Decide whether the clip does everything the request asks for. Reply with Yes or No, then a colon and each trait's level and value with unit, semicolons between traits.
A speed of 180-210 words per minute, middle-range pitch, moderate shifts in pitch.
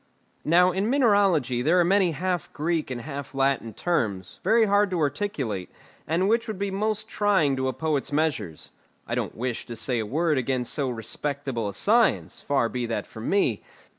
No: average, 185 wpm; medium, 150 Hz; wide, 7.4 semitones